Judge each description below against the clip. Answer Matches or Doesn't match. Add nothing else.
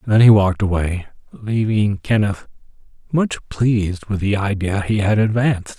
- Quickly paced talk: Doesn't match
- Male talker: Matches